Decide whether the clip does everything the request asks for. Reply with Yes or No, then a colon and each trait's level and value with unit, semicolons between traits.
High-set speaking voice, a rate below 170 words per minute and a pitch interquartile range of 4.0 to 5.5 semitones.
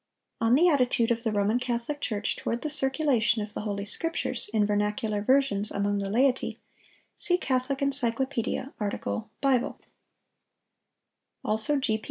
Yes: high, 235 Hz; average, 140 wpm; average, 4.4 semitones